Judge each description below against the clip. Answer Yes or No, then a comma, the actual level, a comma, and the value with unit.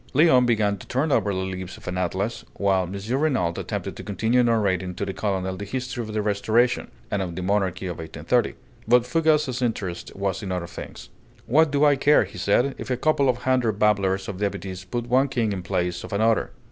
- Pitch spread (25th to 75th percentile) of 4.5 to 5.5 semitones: Yes, average, 4.8 semitones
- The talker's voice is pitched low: Yes, low, 105 Hz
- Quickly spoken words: Yes, fast, 210 wpm